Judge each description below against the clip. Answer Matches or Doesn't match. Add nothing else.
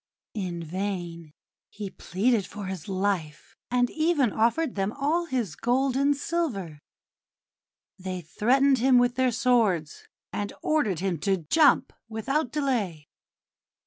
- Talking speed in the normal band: Doesn't match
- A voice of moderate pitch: Doesn't match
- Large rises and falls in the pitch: Matches